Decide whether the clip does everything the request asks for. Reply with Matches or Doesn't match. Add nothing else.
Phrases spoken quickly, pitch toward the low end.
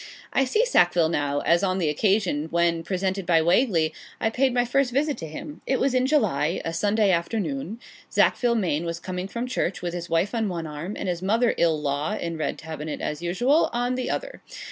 Doesn't match